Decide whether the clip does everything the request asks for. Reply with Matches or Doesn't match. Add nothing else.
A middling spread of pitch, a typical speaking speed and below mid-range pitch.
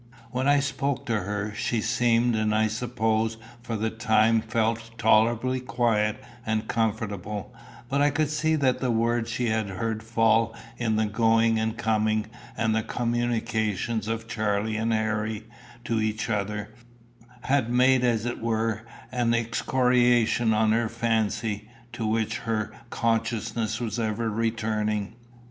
Doesn't match